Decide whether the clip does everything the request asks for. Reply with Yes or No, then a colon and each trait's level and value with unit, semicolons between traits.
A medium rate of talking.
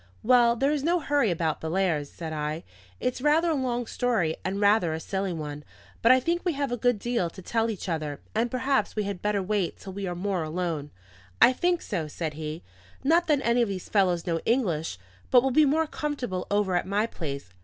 No: fast, 220 wpm